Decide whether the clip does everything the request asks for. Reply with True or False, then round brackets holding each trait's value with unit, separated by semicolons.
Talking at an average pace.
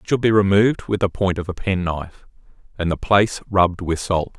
False (220 wpm)